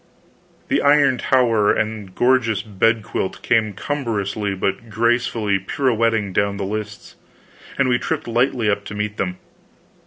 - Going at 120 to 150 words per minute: Yes, slow, 135 wpm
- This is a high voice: No, low, 110 Hz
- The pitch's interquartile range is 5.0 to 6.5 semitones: No, average, 2.9 semitones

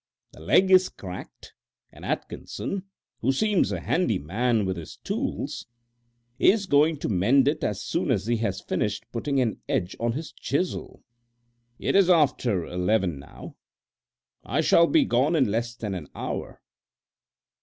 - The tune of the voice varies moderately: No, wide, 8.0 semitones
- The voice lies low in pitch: Yes, low, 120 Hz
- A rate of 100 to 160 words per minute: Yes, average, 155 wpm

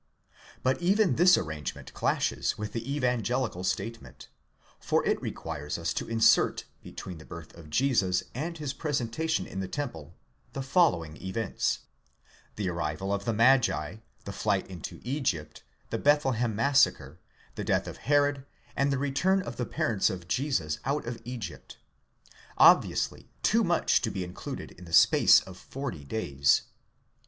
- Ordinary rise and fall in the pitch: No, wide, 7.6 semitones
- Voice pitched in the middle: No, low, 115 Hz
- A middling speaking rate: Yes, average, 155 wpm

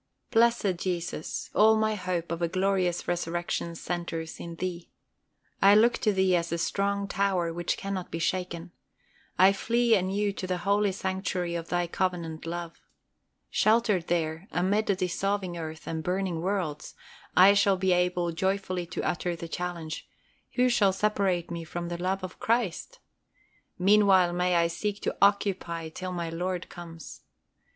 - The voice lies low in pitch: No, medium, 180 Hz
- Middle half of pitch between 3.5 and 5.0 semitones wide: No, narrow, 2.6 semitones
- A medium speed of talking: Yes, average, 155 wpm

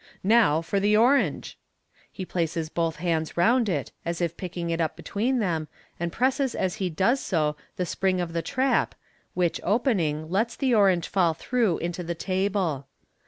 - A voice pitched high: No, medium, 180 Hz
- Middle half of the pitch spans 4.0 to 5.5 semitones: Yes, average, 4.3 semitones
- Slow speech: No, average, 170 wpm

